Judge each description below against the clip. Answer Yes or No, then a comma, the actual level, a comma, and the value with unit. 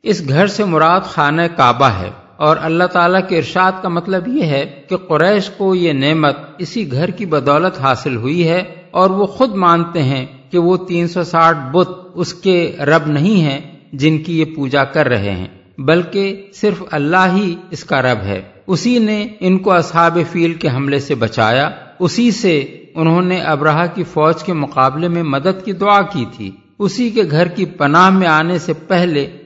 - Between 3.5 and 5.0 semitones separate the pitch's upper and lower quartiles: Yes, average, 4.3 semitones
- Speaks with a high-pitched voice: No, medium, 170 Hz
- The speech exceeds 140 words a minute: Yes, average, 185 wpm